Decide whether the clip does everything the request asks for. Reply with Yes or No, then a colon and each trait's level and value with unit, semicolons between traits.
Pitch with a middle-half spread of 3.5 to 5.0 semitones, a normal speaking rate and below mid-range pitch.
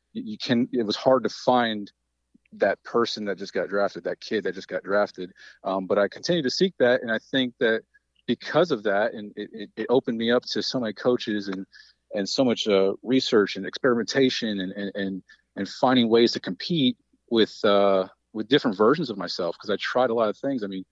No: average, 4.5 semitones; fast, 215 wpm; low, 110 Hz